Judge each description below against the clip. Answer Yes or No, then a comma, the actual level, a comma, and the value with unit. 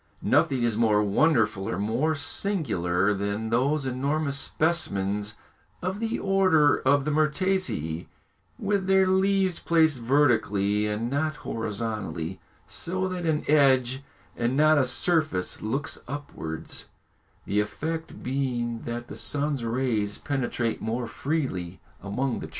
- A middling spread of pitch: No, wide, 6.5 semitones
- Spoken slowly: Yes, slow, 125 wpm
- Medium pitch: No, low, 130 Hz